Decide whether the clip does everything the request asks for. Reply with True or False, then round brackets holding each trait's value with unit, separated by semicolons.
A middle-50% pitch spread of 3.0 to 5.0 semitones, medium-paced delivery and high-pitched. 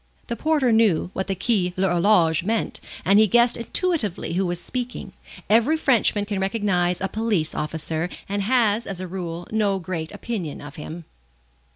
True (4.5 semitones; 165 wpm; 195 Hz)